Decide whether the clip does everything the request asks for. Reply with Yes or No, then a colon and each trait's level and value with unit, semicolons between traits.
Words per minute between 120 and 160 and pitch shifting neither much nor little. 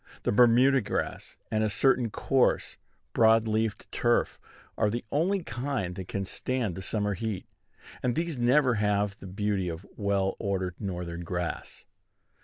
Yes: average, 150 wpm; average, 4.1 semitones